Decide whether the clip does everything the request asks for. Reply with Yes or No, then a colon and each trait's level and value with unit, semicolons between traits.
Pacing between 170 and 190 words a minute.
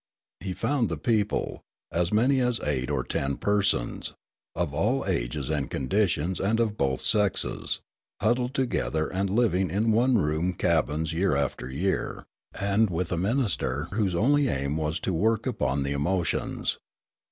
No: average, 150 wpm